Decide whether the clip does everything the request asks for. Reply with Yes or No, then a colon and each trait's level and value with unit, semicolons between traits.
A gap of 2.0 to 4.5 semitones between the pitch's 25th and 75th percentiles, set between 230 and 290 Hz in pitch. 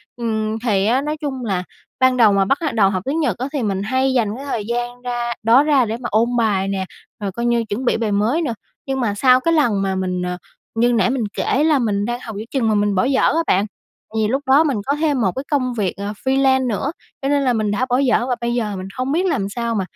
Yes: average, 4.2 semitones; high, 240 Hz